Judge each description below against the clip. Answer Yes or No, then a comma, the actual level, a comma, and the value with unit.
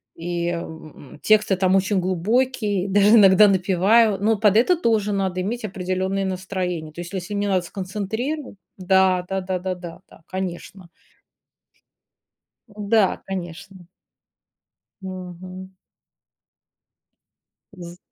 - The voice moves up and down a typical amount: No, narrow, 2.3 semitones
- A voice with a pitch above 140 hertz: Yes, high, 190 Hz